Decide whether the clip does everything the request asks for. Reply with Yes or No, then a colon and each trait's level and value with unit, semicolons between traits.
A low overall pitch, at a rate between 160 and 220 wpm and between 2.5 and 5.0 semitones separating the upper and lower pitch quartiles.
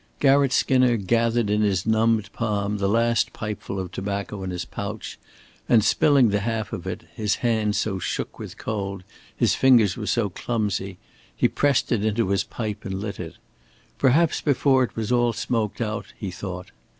Yes: low, 110 Hz; average, 175 wpm; average, 3.0 semitones